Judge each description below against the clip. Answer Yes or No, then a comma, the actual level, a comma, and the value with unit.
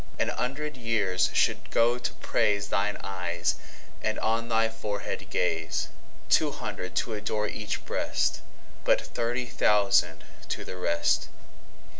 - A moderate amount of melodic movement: Yes, average, 3.2 semitones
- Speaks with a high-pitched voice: No, low, 105 Hz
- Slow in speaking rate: Yes, slow, 115 wpm